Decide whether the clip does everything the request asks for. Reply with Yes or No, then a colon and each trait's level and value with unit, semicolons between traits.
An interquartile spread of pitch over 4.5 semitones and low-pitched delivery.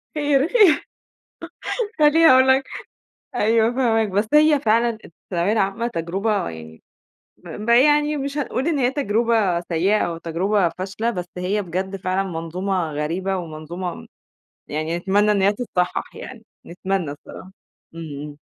No: wide, 5.6 semitones; high, 195 Hz